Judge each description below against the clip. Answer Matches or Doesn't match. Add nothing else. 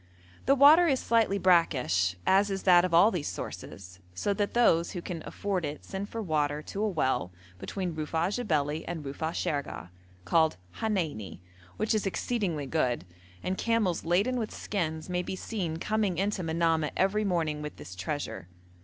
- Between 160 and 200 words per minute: Matches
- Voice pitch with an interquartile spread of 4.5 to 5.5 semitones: Matches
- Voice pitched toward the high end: Doesn't match